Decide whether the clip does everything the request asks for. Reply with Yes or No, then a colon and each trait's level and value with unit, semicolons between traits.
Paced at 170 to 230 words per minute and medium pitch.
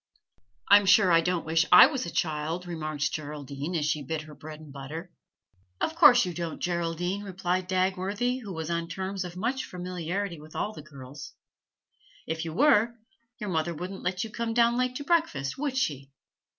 Yes: average, 185 wpm; medium, 175 Hz